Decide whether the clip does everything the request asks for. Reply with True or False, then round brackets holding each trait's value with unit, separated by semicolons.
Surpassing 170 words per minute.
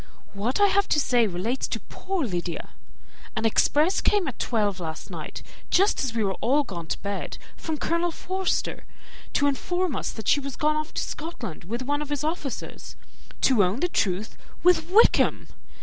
True (180 wpm)